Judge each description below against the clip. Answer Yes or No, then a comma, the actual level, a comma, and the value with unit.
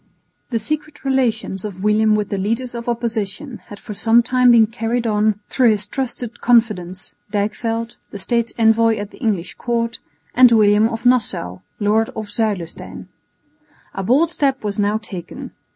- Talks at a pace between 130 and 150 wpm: No, average, 160 wpm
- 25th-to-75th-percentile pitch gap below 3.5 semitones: Yes, narrow, 2.5 semitones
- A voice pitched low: No, high, 225 Hz